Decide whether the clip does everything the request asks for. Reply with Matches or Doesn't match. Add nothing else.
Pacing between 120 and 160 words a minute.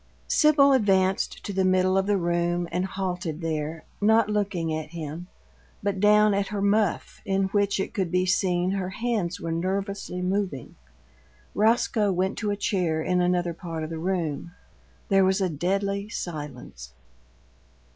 Matches